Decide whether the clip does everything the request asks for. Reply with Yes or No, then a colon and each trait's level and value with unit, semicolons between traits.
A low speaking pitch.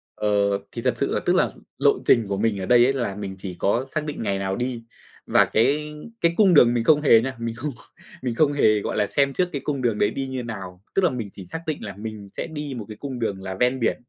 Yes: low, 120 Hz